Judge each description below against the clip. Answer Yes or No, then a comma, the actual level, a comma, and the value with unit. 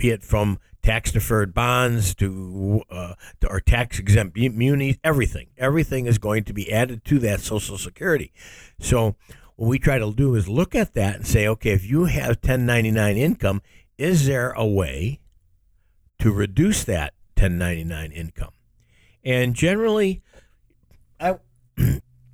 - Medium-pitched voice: No, low, 110 Hz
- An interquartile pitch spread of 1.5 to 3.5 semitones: No, average, 4.7 semitones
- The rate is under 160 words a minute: Yes, average, 145 wpm